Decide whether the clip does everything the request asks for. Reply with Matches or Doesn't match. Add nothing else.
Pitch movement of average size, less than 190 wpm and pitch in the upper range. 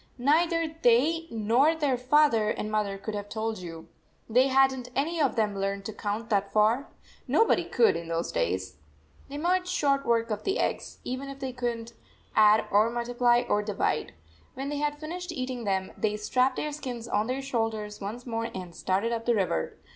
Doesn't match